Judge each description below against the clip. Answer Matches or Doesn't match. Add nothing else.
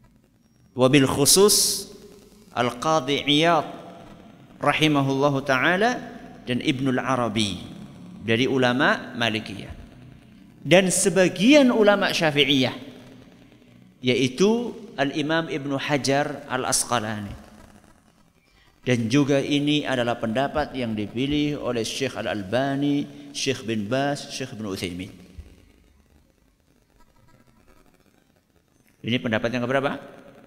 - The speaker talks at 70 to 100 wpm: Matches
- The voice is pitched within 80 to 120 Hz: Doesn't match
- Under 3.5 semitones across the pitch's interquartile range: Doesn't match